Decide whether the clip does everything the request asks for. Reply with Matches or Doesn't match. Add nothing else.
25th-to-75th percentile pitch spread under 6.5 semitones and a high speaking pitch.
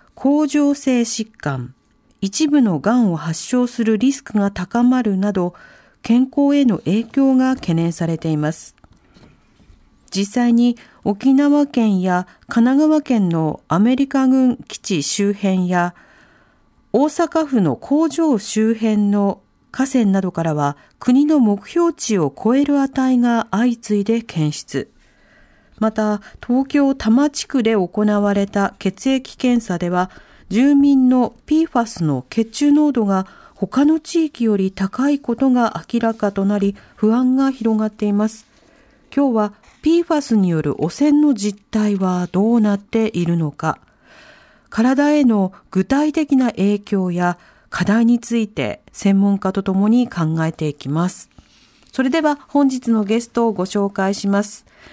Matches